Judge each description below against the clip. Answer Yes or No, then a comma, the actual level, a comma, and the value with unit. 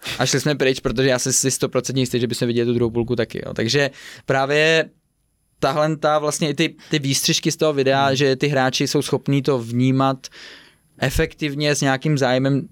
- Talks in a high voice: No, low, 135 Hz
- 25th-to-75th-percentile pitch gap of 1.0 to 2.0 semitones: No, narrow, 2.5 semitones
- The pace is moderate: No, fast, 190 wpm